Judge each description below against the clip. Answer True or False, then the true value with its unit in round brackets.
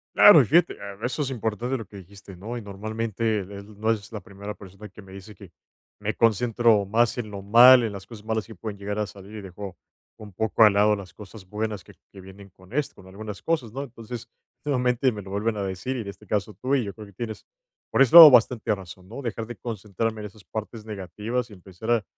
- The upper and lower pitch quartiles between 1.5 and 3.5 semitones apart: True (2.8 semitones)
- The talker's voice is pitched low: True (105 Hz)